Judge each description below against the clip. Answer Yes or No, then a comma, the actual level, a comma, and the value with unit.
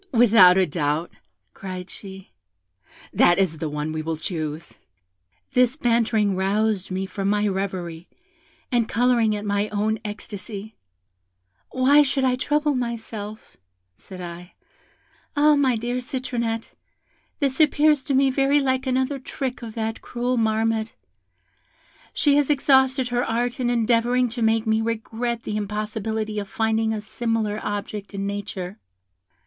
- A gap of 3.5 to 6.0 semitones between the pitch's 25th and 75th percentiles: Yes, average, 3.8 semitones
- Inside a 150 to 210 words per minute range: No, average, 140 wpm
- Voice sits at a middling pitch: No, high, 220 Hz